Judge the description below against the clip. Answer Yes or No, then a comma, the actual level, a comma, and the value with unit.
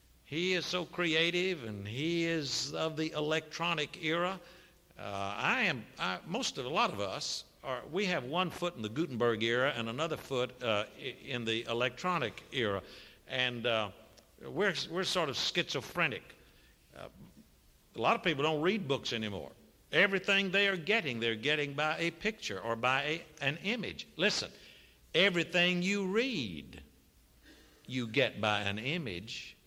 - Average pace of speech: Yes, average, 155 wpm